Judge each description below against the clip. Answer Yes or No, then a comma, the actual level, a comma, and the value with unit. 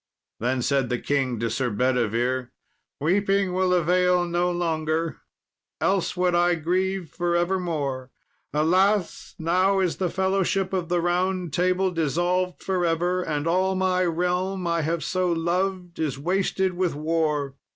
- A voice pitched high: No, medium, 175 Hz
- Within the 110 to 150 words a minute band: Yes, average, 140 wpm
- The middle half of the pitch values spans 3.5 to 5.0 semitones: No, average, 2.7 semitones